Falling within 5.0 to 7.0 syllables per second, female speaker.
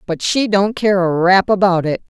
No: 4.7 syllables/s; female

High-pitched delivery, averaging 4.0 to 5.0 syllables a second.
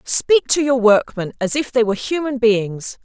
Yes: high, 240 Hz; 4.6 syllables/s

